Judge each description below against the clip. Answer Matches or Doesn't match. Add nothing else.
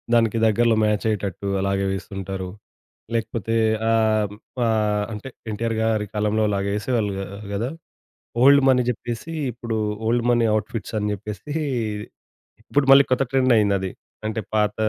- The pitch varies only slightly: Matches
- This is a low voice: Matches